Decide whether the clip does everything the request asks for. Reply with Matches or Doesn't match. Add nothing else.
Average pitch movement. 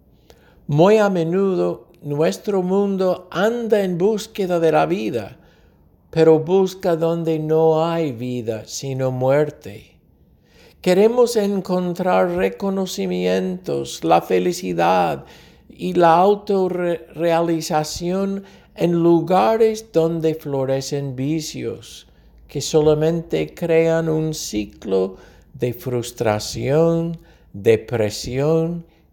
Doesn't match